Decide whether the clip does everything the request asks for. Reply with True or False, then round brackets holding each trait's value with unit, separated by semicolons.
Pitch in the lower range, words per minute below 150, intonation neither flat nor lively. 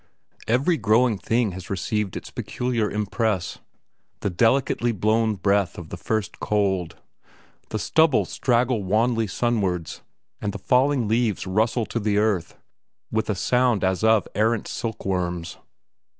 True (110 Hz; 135 wpm; 3.2 semitones)